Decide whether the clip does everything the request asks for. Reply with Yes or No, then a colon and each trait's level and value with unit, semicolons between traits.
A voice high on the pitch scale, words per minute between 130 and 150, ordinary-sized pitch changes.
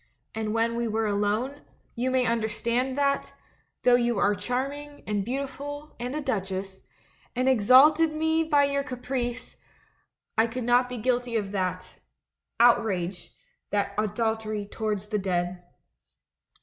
Yes: high, 235 Hz; average, 140 wpm; average, 3.8 semitones